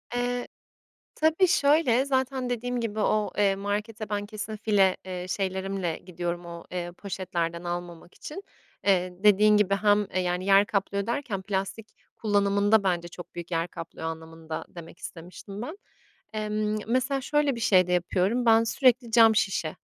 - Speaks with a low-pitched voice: No, high, 200 Hz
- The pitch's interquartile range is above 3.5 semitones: Yes, average, 4.1 semitones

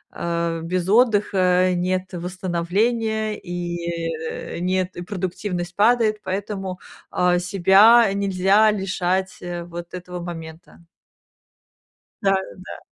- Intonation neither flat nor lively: No, narrow, 2.3 semitones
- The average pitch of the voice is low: No, medium, 185 Hz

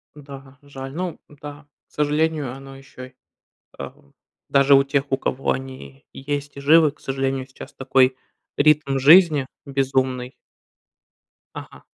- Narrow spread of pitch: Yes, narrow, 1.6 semitones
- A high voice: No, low, 135 Hz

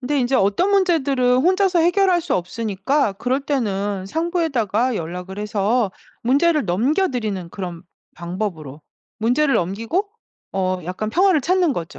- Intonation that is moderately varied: No, wide, 8.5 semitones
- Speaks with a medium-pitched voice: No, high, 240 Hz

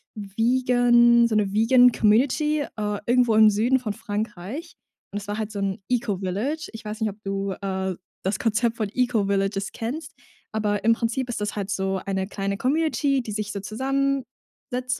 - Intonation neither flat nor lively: Yes, average, 3.6 semitones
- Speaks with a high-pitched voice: Yes, high, 220 Hz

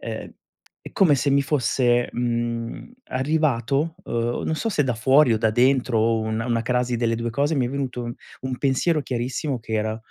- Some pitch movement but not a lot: Yes, average, 3.1 semitones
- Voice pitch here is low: Yes, low, 125 Hz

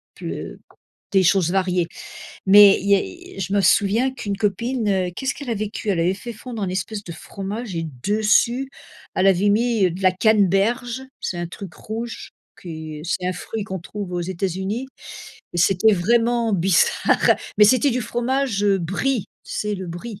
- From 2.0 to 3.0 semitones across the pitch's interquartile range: No, average, 3.7 semitones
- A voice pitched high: Yes, high, 200 Hz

